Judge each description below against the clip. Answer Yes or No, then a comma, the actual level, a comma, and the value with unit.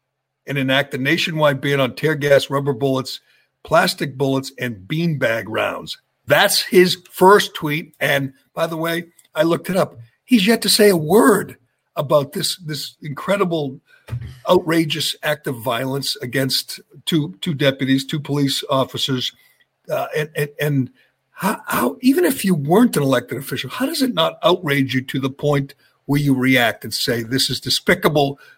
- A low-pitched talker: No, medium, 145 Hz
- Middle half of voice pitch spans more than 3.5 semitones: Yes, average, 4.1 semitones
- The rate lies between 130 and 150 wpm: No, average, 165 wpm